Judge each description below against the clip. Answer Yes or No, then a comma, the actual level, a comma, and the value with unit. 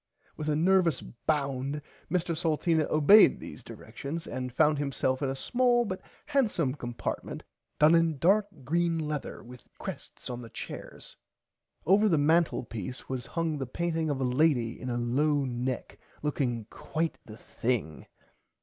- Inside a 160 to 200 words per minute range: No, average, 150 wpm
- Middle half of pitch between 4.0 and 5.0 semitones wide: Yes, average, 4.7 semitones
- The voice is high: No, medium, 150 Hz